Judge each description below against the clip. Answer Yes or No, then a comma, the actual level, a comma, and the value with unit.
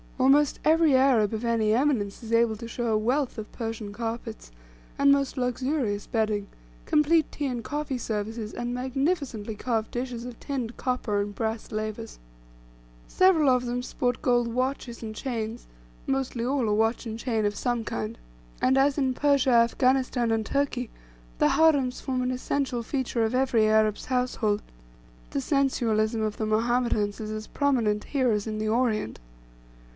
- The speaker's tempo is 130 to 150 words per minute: No, average, 160 wpm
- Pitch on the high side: Yes, high, 240 Hz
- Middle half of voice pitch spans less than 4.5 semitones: Yes, average, 3.3 semitones